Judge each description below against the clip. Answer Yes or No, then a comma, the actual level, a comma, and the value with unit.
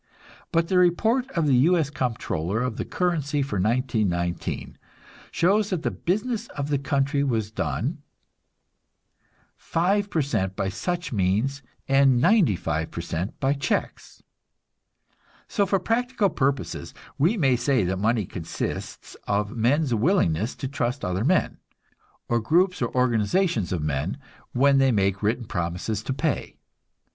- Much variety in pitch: Yes, wide, 8.2 semitones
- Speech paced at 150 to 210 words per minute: No, slow, 135 wpm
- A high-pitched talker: No, low, 130 Hz